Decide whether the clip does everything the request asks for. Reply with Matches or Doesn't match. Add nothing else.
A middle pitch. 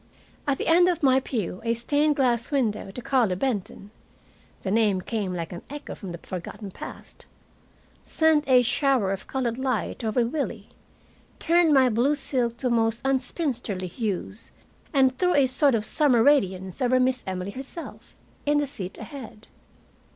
Doesn't match